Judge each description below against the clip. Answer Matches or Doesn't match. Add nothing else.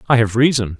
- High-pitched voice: Doesn't match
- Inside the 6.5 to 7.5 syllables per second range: Matches